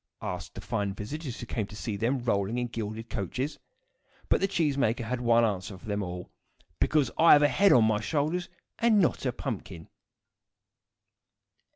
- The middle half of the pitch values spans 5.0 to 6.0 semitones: Yes, wide, 5.6 semitones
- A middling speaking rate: Yes, average, 180 wpm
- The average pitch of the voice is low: Yes, low, 115 Hz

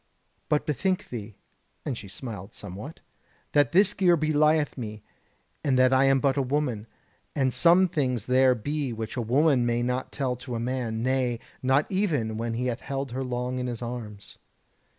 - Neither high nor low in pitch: No, low, 130 Hz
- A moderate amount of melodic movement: Yes, average, 3.7 semitones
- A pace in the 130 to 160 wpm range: No, average, 180 wpm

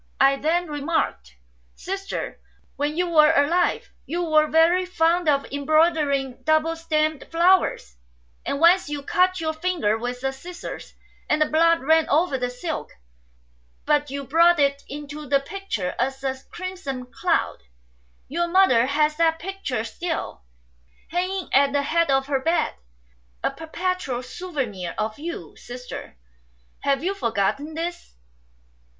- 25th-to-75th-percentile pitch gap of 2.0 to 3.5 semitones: No, average, 4.0 semitones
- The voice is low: No, very high, 305 Hz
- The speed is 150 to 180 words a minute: No, average, 140 wpm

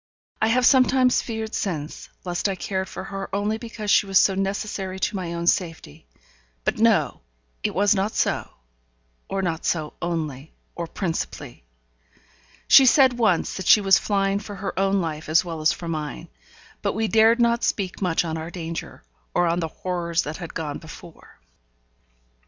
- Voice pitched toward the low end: No, high, 190 Hz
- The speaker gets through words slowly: No, average, 175 wpm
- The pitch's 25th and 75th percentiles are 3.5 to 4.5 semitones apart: Yes, average, 4.0 semitones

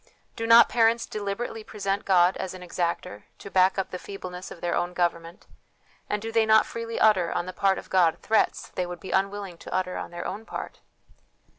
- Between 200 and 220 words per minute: Yes, fast, 205 wpm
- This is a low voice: No, high, 190 Hz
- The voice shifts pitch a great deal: No, average, 3.3 semitones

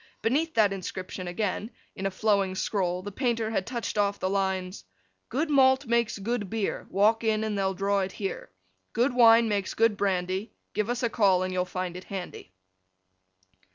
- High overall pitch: Yes, high, 205 Hz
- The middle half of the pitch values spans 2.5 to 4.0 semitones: Yes, average, 3.3 semitones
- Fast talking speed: No, average, 180 wpm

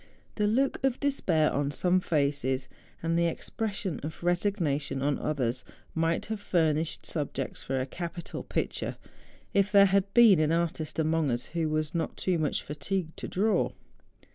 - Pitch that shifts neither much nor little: Yes, average, 4.6 semitones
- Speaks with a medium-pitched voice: Yes, medium, 165 Hz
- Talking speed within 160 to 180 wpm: Yes, average, 165 wpm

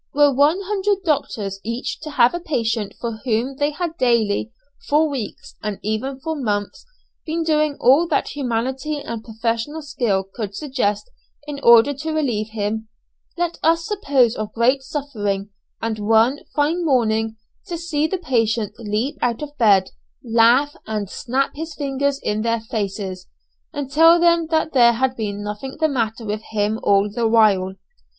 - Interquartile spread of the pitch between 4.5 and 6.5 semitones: Yes, average, 5.3 semitones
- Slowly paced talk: No, average, 160 wpm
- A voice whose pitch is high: Yes, high, 245 Hz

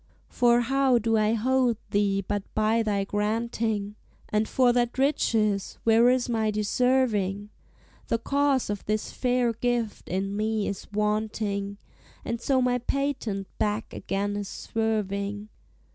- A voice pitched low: No, high, 220 Hz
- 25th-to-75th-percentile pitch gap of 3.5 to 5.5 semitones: No, average, 2.9 semitones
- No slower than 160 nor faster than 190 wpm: No, slow, 135 wpm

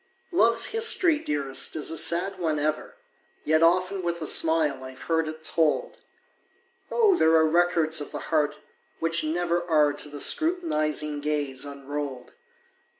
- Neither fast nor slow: Yes, average, 150 wpm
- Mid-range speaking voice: Yes, medium, 160 Hz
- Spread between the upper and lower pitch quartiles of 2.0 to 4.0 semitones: Yes, average, 2.9 semitones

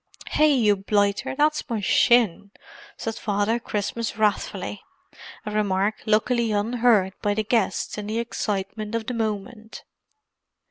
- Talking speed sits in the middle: No, slow, 130 wpm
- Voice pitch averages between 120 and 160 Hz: No, high, 215 Hz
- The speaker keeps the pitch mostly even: Yes, narrow, 2.3 semitones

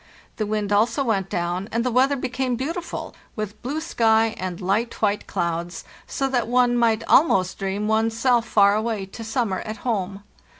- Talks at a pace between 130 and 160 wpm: No, average, 175 wpm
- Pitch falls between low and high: No, high, 220 Hz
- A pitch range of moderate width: Yes, average, 3.4 semitones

